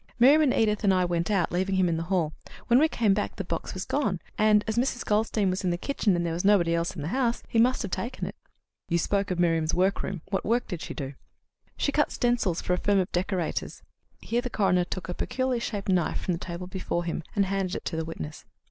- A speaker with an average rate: No, fast, 250 wpm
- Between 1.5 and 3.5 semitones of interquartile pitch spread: No, average, 4.2 semitones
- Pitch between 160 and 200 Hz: Yes, high, 190 Hz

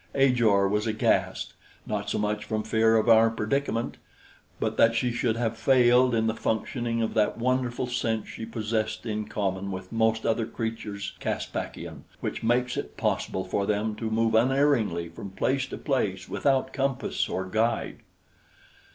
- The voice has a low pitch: Yes, low, 110 Hz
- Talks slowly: No, average, 160 wpm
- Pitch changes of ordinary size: No, narrow, 2.3 semitones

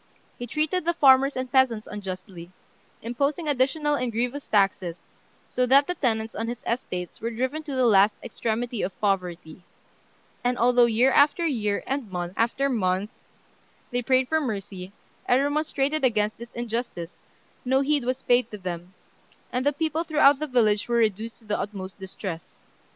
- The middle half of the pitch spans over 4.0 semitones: Yes, average, 4.7 semitones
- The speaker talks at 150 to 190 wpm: Yes, average, 165 wpm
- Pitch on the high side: Yes, high, 240 Hz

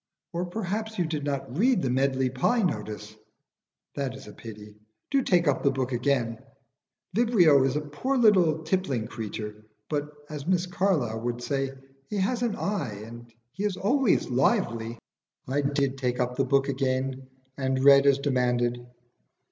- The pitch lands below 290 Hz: Yes, medium, 140 Hz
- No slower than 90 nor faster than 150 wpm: No, average, 165 wpm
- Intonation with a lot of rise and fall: Yes, wide, 6.2 semitones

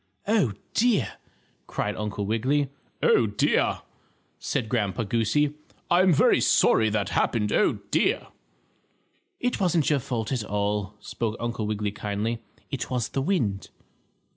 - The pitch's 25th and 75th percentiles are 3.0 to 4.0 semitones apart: No, average, 5.0 semitones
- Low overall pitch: Yes, low, 115 Hz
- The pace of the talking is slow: Yes, slow, 130 wpm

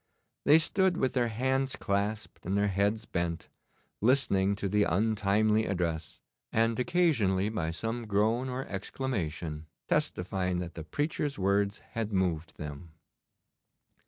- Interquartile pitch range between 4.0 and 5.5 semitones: Yes, average, 4.5 semitones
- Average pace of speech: No, slow, 130 wpm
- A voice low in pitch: Yes, low, 100 Hz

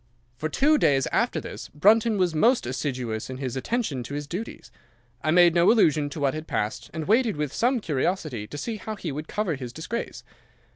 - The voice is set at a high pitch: No, medium, 155 Hz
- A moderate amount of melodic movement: No, wide, 7.7 semitones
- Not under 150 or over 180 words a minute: No, average, 200 wpm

